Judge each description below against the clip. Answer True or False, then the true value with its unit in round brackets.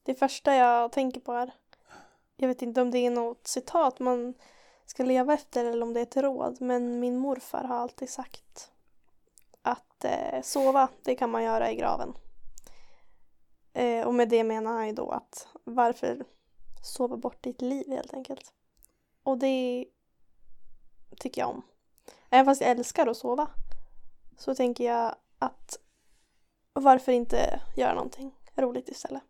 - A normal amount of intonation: False (1.7 semitones)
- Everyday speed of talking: True (150 wpm)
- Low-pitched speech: False (250 Hz)